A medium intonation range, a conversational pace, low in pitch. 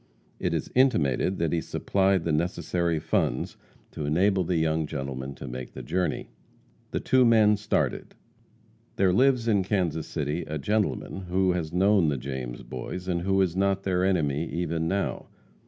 Yes: average, 3.9 semitones; average, 165 wpm; very low, 85 Hz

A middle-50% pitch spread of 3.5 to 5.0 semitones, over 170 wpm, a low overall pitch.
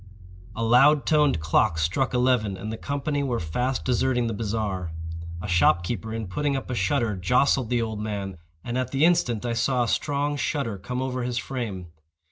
Yes: average, 4.3 semitones; average, 190 wpm; low, 120 Hz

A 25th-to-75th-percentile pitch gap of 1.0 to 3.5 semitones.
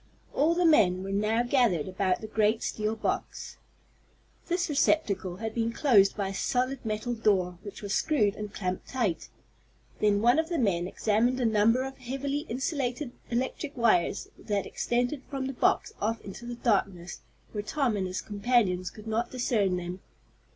No: average, 4.3 semitones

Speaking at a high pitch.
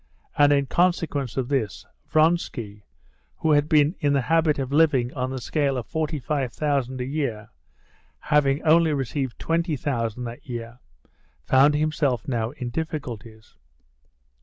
No: medium, 140 Hz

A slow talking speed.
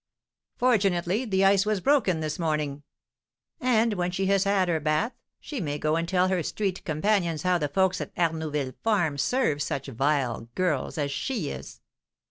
No: average, 170 wpm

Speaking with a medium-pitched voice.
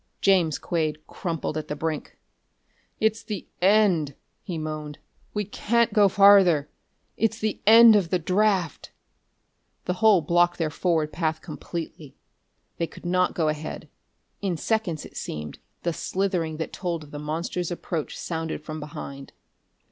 Yes: medium, 170 Hz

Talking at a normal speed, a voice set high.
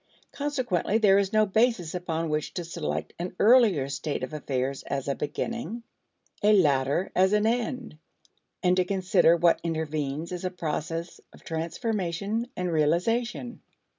No: average, 145 wpm; medium, 180 Hz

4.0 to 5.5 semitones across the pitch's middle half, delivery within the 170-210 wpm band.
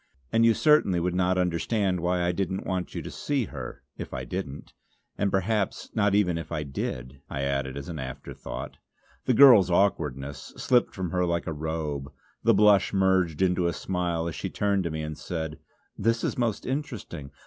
Yes: average, 4.5 semitones; average, 185 wpm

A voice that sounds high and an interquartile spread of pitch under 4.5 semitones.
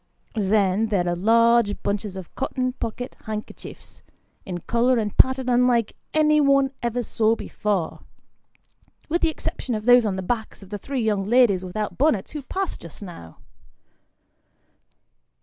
Yes: high, 225 Hz; average, 4.0 semitones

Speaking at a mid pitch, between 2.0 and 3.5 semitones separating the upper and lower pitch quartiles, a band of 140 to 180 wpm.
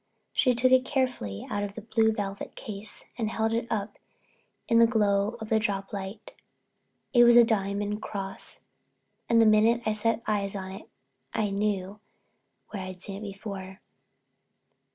No: high, 210 Hz; narrow, 2.4 semitones; average, 165 wpm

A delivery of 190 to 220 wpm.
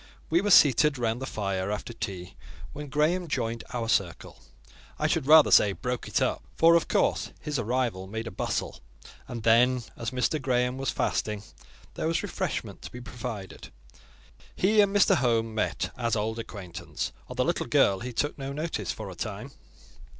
No: average, 175 wpm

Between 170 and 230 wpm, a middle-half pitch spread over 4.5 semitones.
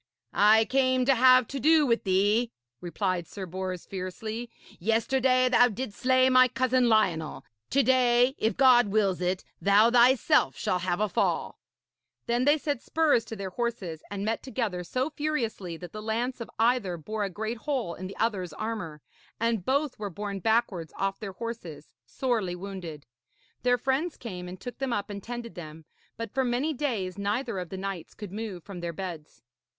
Yes: average, 180 wpm; average, 5.0 semitones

